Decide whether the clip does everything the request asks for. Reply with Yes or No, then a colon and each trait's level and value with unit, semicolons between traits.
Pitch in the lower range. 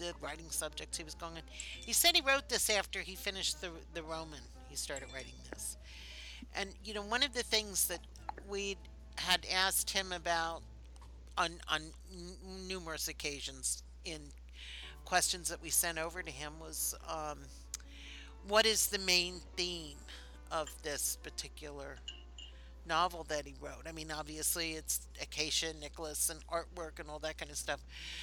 No: medium, 155 Hz